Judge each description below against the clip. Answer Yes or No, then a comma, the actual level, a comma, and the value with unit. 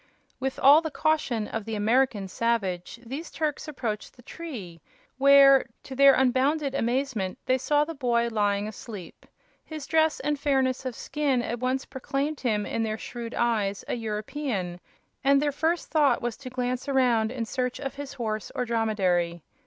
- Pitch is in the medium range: No, very high, 250 Hz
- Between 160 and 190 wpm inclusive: Yes, average, 170 wpm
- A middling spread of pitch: Yes, average, 4.1 semitones